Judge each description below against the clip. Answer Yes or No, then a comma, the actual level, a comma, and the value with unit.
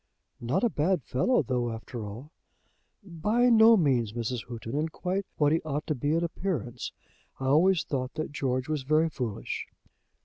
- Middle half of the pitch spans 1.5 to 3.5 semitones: No, average, 5.3 semitones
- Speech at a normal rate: Yes, average, 170 wpm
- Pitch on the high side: No, medium, 145 Hz